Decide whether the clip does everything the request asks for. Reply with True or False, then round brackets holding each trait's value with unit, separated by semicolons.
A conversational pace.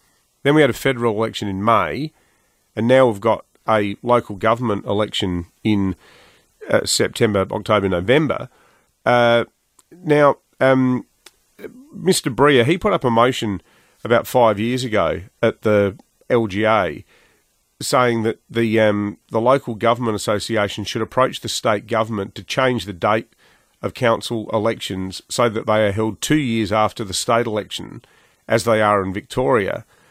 True (145 wpm)